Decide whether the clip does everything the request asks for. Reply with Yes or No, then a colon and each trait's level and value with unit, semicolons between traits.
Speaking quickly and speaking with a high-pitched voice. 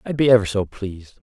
No: fast, 235 wpm; low, 105 Hz